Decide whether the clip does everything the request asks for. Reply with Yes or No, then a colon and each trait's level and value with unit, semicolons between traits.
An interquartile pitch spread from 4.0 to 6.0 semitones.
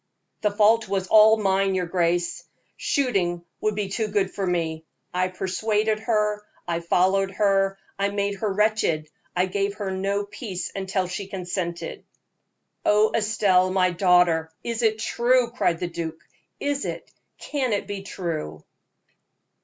No: average, 2.9 semitones